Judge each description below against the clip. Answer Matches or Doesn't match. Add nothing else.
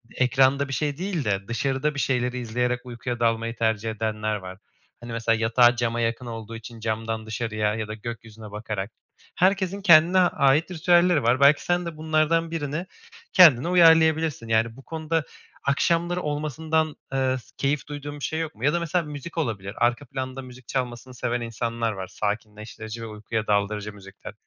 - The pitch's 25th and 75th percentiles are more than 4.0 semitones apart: Matches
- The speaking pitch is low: Matches